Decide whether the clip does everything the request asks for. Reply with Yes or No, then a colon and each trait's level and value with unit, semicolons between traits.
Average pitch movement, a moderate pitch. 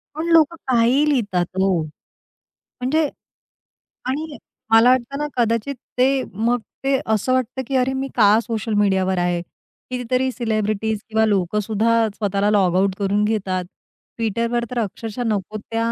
No: average, 3.9 semitones; high, 225 Hz